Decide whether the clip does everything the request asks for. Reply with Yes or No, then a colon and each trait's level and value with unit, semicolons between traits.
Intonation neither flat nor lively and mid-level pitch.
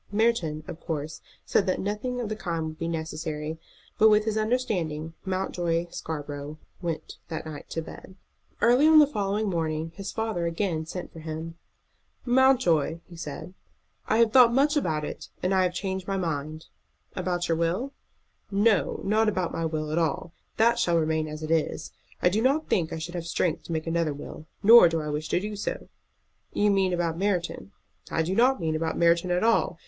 Yes: average, 4.7 semitones; medium, 175 Hz